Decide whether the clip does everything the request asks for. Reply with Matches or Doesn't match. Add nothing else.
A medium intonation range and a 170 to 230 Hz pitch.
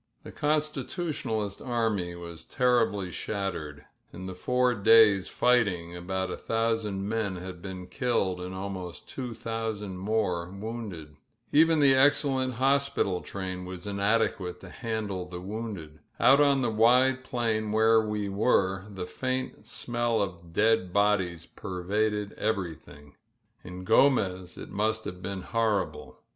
Doesn't match